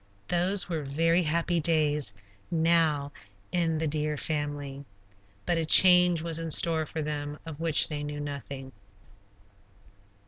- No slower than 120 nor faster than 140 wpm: Yes, slow, 135 wpm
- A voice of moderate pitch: Yes, medium, 155 Hz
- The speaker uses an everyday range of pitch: No, narrow, 2.2 semitones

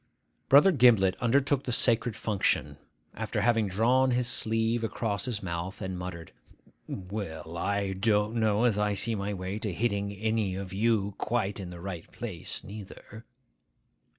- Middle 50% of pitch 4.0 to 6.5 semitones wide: No, average, 3.2 semitones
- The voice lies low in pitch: Yes, low, 105 Hz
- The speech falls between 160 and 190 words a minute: No, average, 150 wpm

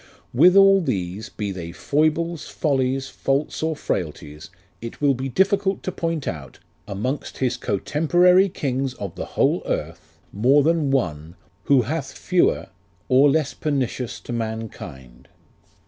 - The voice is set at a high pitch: No, low, 135 Hz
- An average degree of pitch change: No, wide, 7.5 semitones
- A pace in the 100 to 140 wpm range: Yes, slow, 135 wpm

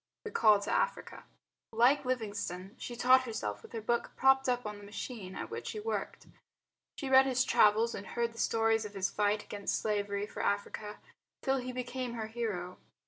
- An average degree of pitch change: Yes, average, 3.5 semitones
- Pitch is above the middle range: Yes, high, 225 Hz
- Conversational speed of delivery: Yes, average, 190 wpm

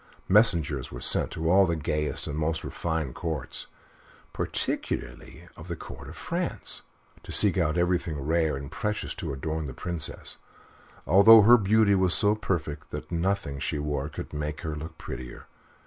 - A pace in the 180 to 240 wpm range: No, average, 165 wpm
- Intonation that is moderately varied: Yes, average, 3.9 semitones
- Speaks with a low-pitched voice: Yes, very low, 80 Hz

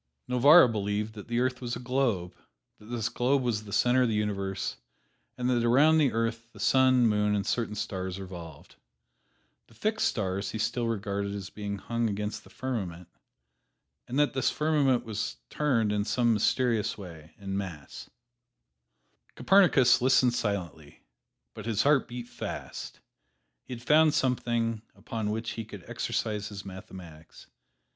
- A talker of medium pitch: No, low, 115 Hz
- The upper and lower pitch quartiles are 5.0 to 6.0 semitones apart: No, average, 3.8 semitones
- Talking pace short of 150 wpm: No, average, 155 wpm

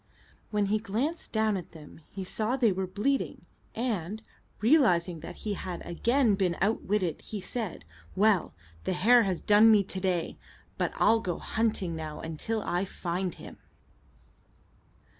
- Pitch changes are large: No, average, 3.8 semitones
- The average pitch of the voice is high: Yes, high, 200 Hz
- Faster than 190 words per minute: No, average, 150 wpm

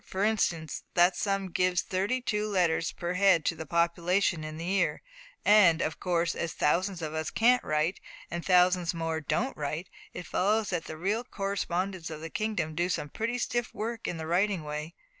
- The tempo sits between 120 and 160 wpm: No, average, 190 wpm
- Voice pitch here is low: No, medium, 180 Hz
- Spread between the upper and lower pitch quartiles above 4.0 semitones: No, average, 3.5 semitones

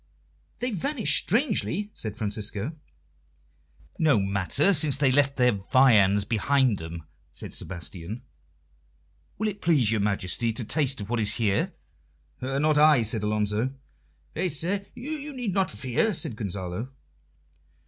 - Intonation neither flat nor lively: No, wide, 7.3 semitones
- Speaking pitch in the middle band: No, low, 125 Hz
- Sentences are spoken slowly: Yes, slow, 130 wpm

